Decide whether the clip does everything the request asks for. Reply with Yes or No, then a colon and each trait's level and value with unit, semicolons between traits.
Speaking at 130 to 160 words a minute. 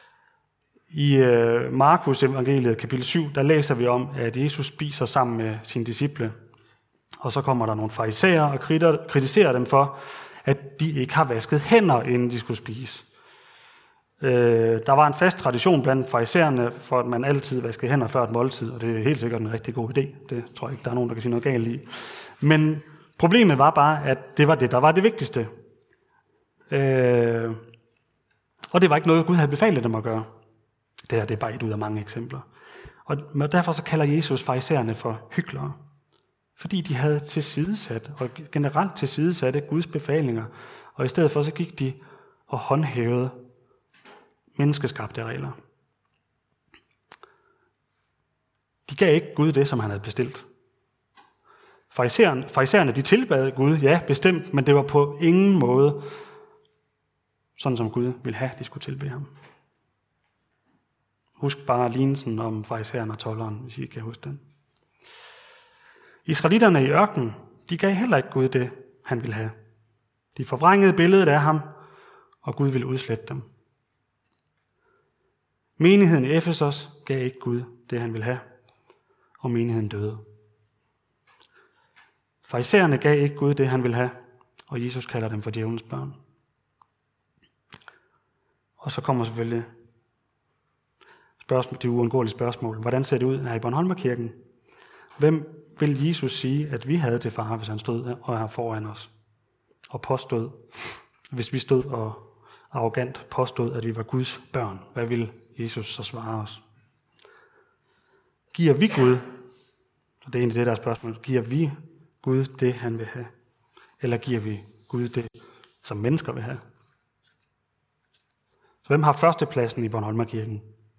Yes: average, 155 wpm